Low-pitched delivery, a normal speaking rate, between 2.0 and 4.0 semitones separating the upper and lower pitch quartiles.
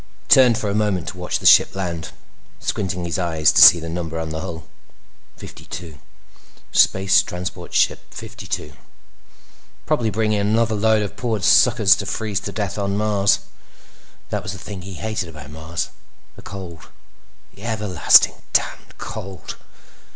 Yes: very low, 95 Hz; average, 160 wpm; average, 3.6 semitones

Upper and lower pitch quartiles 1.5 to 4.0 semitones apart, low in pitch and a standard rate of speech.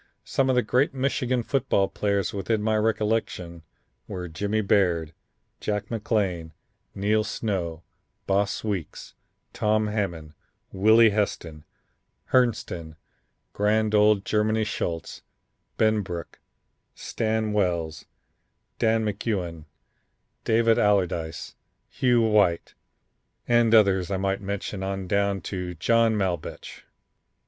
No: average, 3.4 semitones; low, 105 Hz; slow, 105 wpm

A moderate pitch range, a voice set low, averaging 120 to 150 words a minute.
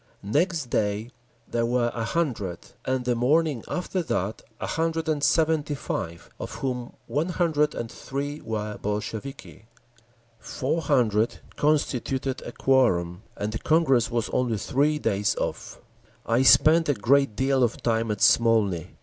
Yes: average, 5.0 semitones; low, 125 Hz; average, 145 wpm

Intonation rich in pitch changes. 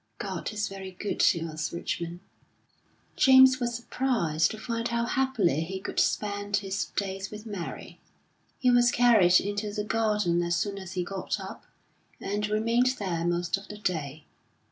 No: average, 4.6 semitones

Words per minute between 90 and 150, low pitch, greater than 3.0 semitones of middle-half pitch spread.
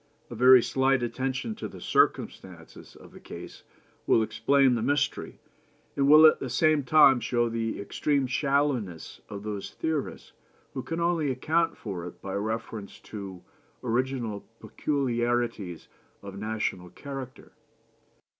Yes: slow, 135 wpm; low, 125 Hz; average, 4.6 semitones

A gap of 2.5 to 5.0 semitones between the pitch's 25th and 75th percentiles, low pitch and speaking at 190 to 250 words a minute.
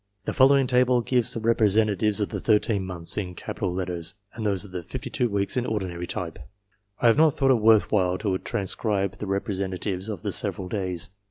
Yes: average, 3.4 semitones; low, 100 Hz; average, 195 wpm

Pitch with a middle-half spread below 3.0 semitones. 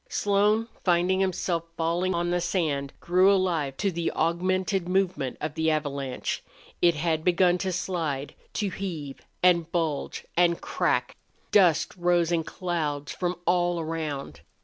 Yes: narrow, 2.6 semitones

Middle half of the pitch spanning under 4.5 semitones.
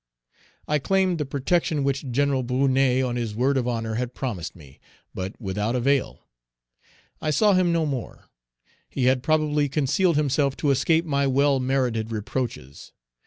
Yes: average, 3.3 semitones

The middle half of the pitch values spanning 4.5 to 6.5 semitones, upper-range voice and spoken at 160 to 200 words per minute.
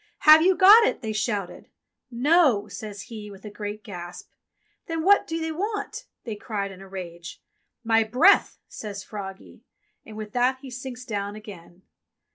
Yes: average, 5.1 semitones; high, 215 Hz; average, 180 wpm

